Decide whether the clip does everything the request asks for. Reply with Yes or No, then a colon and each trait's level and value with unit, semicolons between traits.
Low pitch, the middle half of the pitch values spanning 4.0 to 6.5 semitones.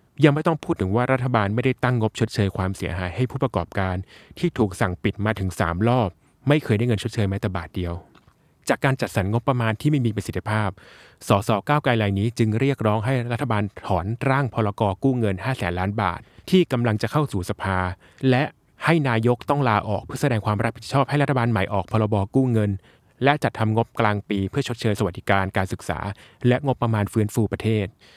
Yes: low, 110 Hz; average, 4.4 semitones